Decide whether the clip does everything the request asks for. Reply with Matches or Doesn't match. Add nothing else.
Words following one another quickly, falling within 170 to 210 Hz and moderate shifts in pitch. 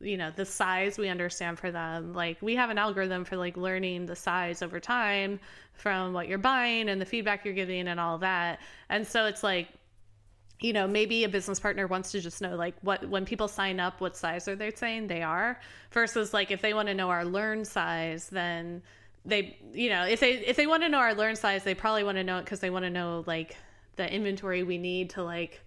Matches